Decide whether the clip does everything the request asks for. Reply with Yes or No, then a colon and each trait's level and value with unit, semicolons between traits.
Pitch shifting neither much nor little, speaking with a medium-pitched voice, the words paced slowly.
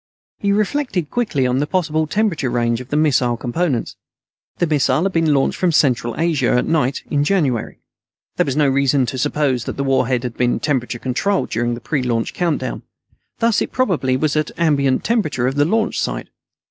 No: average, 4.6 semitones; medium, 145 Hz; average, 195 wpm